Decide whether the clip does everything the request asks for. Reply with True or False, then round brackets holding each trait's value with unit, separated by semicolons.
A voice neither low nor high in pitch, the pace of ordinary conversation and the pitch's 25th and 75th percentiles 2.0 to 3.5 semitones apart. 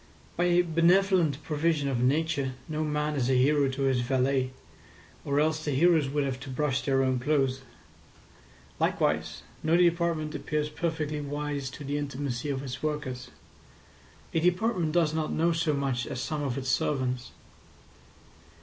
True (145 Hz; 160 wpm; 3.1 semitones)